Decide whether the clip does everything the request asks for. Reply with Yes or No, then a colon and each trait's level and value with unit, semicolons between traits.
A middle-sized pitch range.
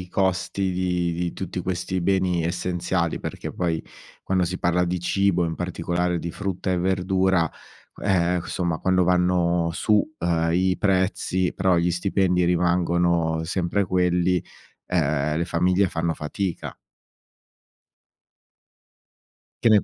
No: narrow, 1.4 semitones